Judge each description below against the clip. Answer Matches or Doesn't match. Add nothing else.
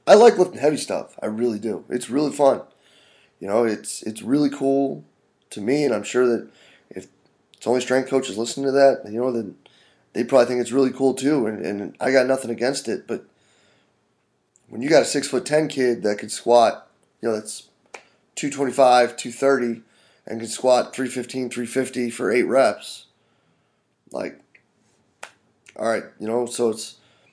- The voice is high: Doesn't match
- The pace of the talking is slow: Doesn't match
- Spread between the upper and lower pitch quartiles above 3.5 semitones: Doesn't match